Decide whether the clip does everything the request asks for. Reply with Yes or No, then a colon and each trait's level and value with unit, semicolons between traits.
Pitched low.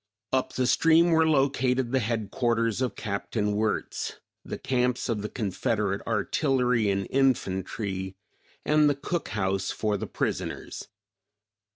Yes: low, 115 Hz